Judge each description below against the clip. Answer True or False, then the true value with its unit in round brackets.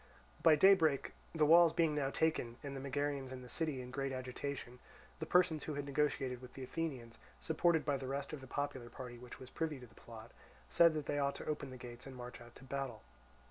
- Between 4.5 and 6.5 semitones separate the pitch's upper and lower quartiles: False (3.3 semitones)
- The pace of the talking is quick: True (225 wpm)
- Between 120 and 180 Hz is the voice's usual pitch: True (140 Hz)